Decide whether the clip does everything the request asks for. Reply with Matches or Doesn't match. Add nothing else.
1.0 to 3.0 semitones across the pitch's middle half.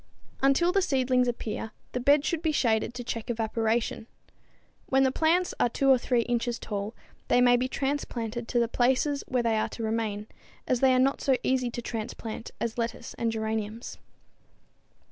Matches